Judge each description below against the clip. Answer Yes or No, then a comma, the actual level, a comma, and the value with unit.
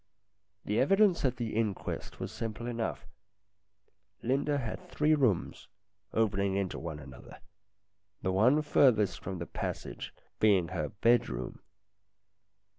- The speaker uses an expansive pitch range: Yes, wide, 5.7 semitones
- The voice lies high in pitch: No, low, 110 Hz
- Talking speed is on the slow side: Yes, slow, 120 wpm